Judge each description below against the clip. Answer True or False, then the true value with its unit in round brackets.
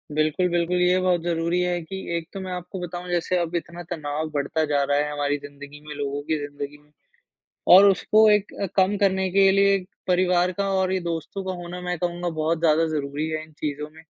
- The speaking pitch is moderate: True (170 Hz)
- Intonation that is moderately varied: True (3.3 semitones)